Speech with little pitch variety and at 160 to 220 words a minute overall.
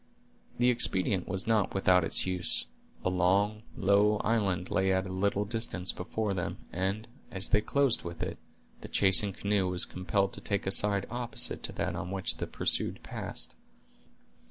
Yes: narrow, 2.2 semitones; average, 170 wpm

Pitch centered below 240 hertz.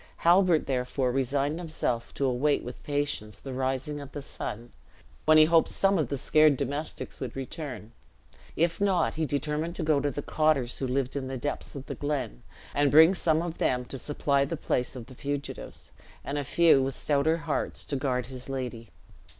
Yes: medium, 140 Hz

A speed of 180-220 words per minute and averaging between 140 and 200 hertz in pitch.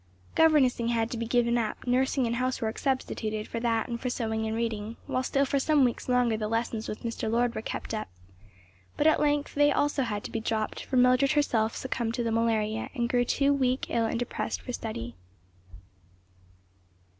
No: average, 195 wpm; high, 235 Hz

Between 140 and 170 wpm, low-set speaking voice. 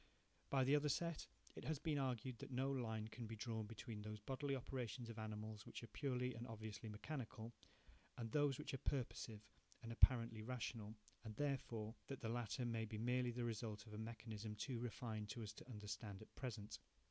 No: average, 195 wpm; low, 115 Hz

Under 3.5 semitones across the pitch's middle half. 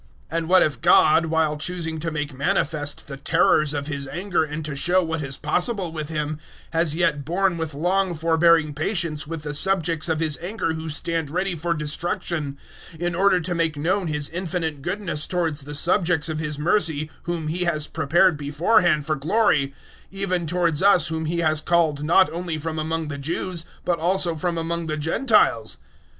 Yes: narrow, 2.5 semitones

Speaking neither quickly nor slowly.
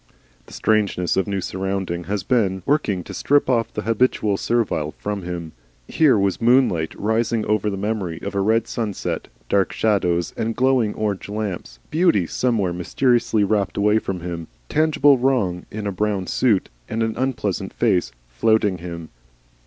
Yes: average, 160 wpm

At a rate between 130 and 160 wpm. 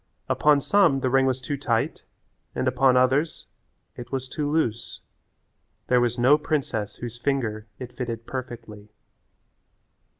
Yes: slow, 135 wpm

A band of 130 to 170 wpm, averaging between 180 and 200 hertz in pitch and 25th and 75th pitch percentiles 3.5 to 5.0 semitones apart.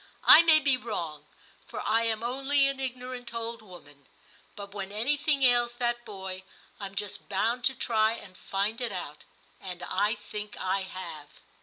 No: average, 165 wpm; high, 220 Hz; average, 4.4 semitones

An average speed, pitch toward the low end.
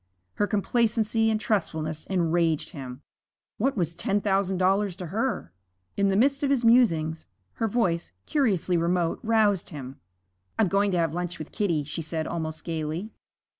No: average, 160 wpm; medium, 185 Hz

